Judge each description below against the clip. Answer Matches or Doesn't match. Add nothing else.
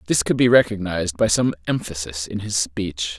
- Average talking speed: Matches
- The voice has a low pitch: Matches